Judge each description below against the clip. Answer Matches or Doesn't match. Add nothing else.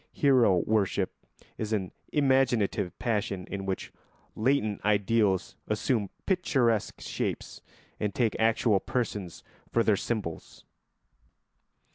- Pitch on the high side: Doesn't match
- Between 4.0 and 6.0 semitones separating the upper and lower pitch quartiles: Doesn't match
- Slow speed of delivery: Matches